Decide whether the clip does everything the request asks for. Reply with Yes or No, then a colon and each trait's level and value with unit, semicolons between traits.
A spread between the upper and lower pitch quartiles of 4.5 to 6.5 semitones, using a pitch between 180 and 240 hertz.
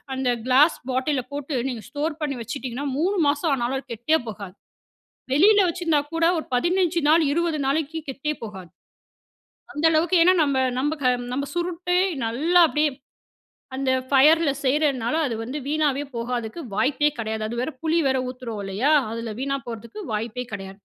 No: average, 4.9 semitones; very high, 280 Hz